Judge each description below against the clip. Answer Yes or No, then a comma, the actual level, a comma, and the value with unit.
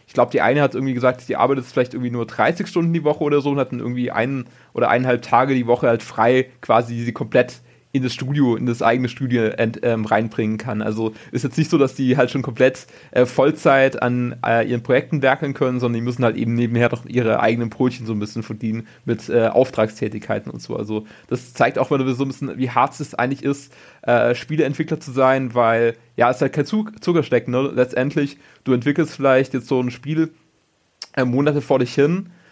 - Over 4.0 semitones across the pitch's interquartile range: No, average, 3.0 semitones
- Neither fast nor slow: No, fast, 220 wpm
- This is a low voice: Yes, low, 125 Hz